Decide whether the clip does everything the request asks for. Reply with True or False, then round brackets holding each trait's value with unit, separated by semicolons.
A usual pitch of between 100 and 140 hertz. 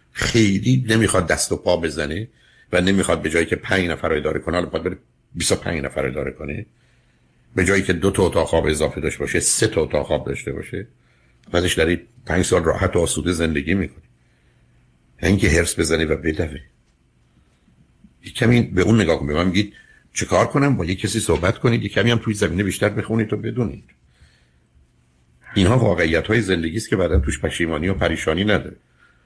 False (90 Hz)